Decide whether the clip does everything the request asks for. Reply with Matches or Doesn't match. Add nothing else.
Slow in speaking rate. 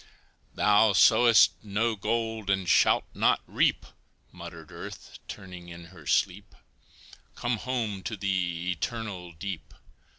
Matches